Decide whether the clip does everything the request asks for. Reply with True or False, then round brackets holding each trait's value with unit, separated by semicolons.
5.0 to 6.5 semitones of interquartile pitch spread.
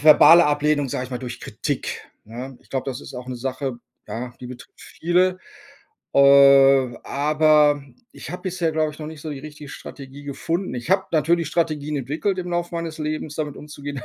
False (2.8 semitones)